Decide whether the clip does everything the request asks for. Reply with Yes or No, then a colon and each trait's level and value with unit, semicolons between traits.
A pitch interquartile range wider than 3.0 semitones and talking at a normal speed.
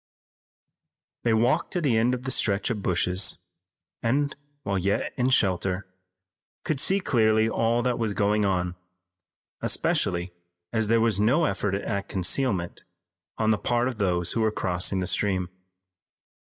Yes: average, 3.9 semitones; average, 150 wpm